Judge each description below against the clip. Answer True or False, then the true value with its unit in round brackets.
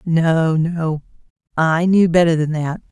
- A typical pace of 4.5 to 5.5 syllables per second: False (3.7 syllables/s)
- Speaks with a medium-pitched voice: True (165 Hz)